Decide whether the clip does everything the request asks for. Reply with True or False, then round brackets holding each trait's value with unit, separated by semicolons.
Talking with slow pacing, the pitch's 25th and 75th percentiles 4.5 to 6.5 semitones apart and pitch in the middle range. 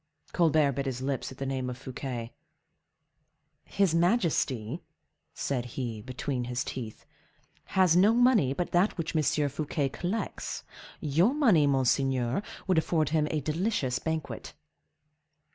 True (130 wpm; 5.1 semitones; 145 Hz)